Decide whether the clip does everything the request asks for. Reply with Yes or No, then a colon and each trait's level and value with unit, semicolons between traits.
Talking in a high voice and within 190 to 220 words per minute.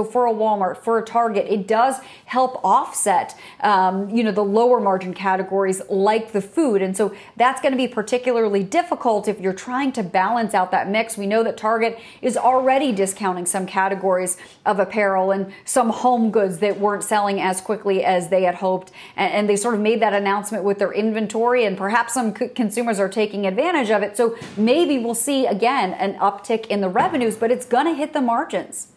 Yes: high, 215 Hz; average, 200 wpm